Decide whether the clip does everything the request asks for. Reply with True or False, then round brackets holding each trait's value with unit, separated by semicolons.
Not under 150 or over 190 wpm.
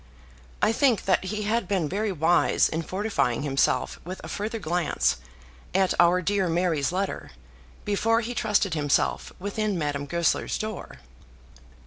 False (140 wpm)